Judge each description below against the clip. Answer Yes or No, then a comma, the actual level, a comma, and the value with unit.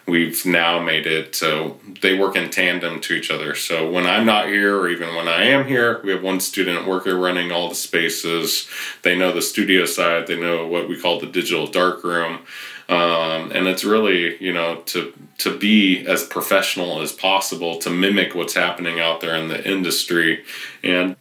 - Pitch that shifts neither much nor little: No, narrow, 2.2 semitones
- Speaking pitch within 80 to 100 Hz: Yes, very low, 90 Hz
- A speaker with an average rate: Yes, average, 195 wpm